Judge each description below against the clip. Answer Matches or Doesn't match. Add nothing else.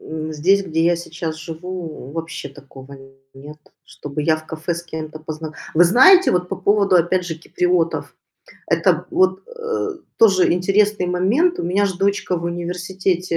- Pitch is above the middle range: Doesn't match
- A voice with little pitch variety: Doesn't match